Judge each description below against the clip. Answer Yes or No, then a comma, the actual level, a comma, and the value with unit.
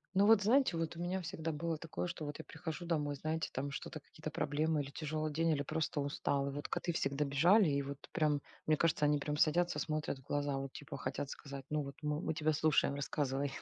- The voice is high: No, medium, 150 Hz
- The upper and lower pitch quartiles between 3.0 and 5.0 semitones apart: No, narrow, 2.4 semitones